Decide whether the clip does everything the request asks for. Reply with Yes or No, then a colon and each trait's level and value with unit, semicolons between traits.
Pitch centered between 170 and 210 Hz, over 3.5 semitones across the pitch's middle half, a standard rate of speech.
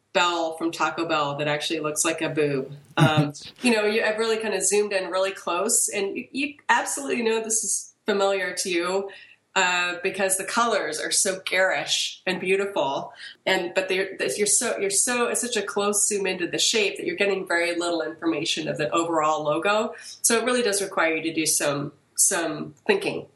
Yes: high, 190 Hz; average, 4.3 semitones; average, 195 wpm